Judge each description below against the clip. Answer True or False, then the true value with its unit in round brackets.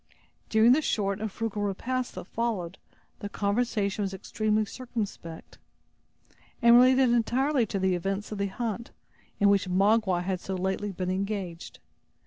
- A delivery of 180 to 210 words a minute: False (145 wpm)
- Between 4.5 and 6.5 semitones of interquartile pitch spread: False (3.4 semitones)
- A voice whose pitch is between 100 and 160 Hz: False (205 Hz)